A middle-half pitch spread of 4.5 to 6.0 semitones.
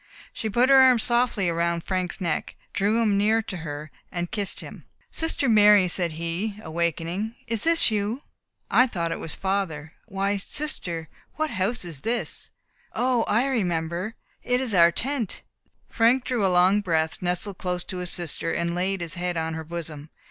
Yes: average, 4.9 semitones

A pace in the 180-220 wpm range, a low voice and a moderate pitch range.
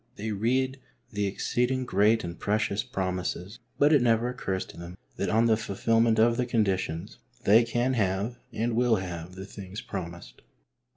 No: average, 165 wpm; low, 110 Hz; average, 3.8 semitones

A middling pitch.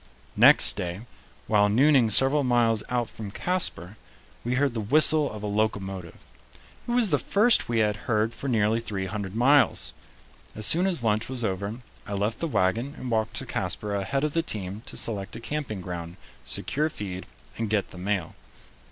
No: low, 110 Hz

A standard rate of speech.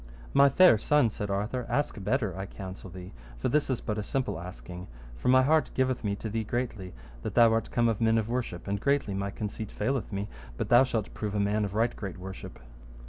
No: fast, 225 wpm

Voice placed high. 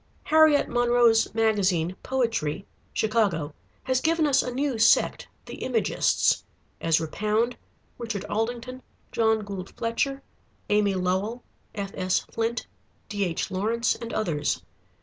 Yes: high, 225 Hz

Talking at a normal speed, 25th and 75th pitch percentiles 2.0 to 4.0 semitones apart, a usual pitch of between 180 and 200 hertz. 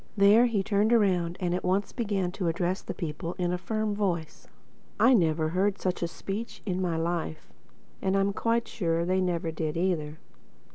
Yes: average, 190 wpm; average, 3.1 semitones; medium, 185 Hz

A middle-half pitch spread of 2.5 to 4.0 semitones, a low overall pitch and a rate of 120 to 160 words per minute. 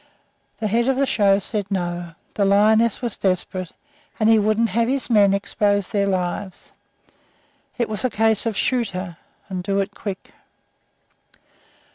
No: average, 2.8 semitones; high, 205 Hz; average, 155 wpm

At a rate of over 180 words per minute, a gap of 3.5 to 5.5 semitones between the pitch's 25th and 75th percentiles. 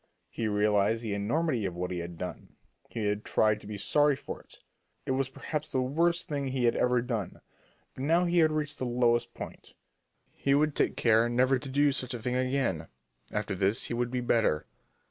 Yes: fast, 205 wpm; average, 4.5 semitones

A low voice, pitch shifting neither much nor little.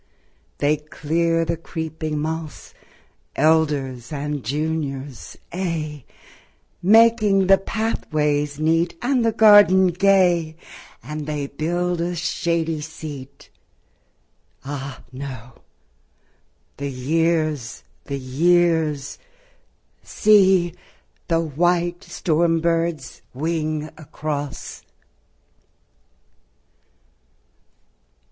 No: medium, 160 Hz; average, 3.1 semitones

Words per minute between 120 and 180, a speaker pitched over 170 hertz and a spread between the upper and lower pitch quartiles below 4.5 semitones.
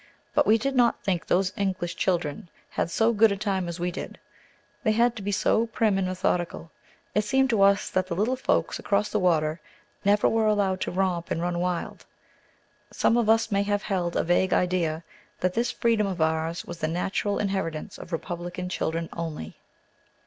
No: average, 190 wpm; high, 190 Hz; average, 3.4 semitones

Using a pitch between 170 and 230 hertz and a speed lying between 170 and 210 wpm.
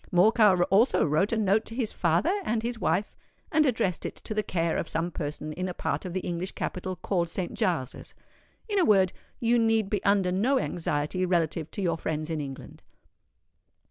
Yes: medium, 185 Hz; average, 195 wpm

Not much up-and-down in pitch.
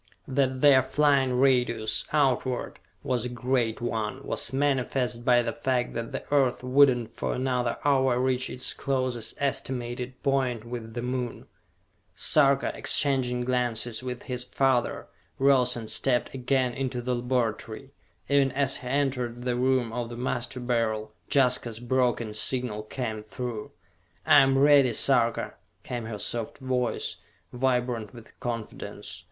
Yes: narrow, 1.8 semitones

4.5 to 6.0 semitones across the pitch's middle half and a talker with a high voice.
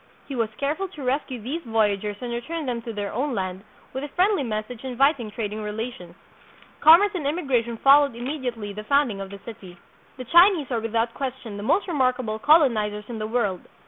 Yes: average, 4.8 semitones; high, 240 Hz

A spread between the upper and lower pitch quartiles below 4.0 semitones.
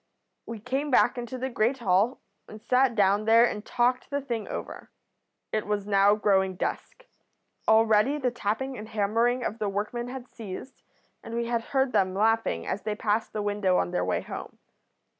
Yes: average, 3.1 semitones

